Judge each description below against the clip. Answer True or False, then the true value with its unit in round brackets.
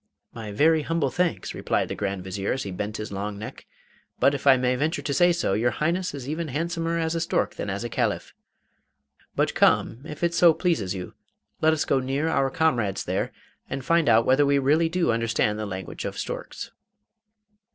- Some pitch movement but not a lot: False (7.1 semitones)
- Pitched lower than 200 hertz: True (140 Hz)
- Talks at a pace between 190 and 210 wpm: True (205 wpm)